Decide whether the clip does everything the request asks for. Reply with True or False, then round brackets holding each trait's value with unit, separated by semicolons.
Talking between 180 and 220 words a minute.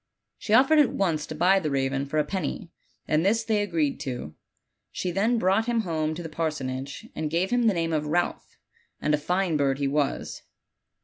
True (200 wpm)